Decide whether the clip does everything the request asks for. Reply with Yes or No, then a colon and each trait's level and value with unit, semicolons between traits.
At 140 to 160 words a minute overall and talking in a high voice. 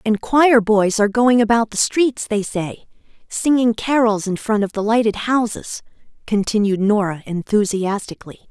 Yes: average, 150 wpm; high, 215 Hz